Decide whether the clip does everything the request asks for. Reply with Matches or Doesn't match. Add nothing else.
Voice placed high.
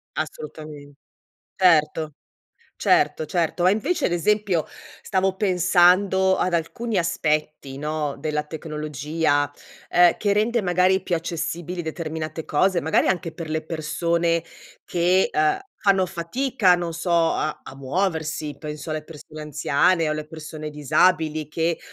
Doesn't match